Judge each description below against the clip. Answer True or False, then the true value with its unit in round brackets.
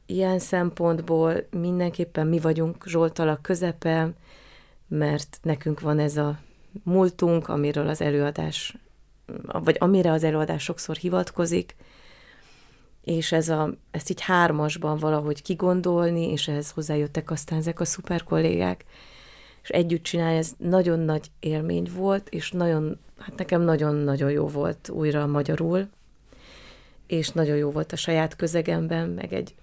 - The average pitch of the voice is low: False (160 Hz)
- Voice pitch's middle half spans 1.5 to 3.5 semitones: True (2.5 semitones)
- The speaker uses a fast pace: False (130 wpm)